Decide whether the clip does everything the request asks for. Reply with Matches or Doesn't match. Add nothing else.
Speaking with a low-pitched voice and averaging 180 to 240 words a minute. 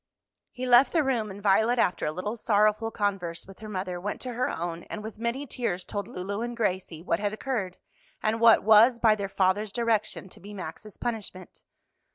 Doesn't match